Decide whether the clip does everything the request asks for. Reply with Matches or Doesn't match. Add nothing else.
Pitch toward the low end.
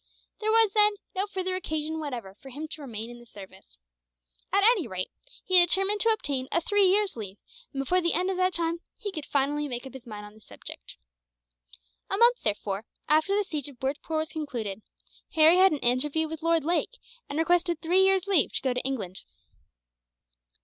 Doesn't match